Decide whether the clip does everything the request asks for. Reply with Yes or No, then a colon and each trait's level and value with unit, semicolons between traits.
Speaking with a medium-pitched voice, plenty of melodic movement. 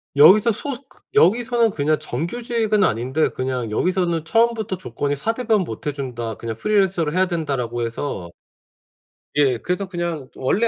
Yes: medium, 165 Hz; wide, 8.1 semitones